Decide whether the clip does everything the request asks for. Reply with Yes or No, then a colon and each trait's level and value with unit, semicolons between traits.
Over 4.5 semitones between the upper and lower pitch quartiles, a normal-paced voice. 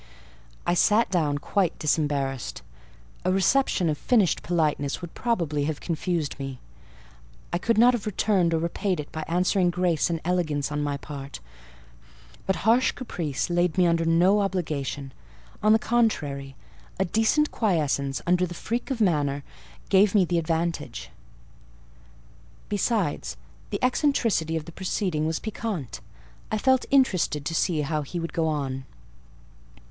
Yes: average, 5.2 semitones; average, 145 wpm